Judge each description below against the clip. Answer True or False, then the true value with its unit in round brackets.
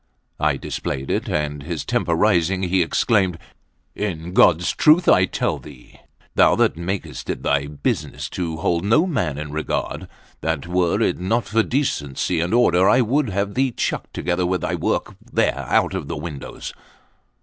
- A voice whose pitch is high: False (90 Hz)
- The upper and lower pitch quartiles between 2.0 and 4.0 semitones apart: False (4.7 semitones)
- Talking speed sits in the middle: True (165 wpm)